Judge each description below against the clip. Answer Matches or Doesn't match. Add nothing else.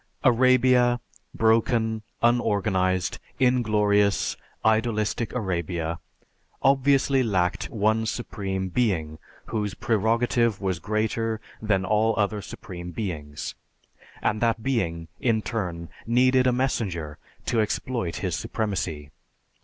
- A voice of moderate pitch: Doesn't match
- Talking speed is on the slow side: Matches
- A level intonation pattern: Doesn't match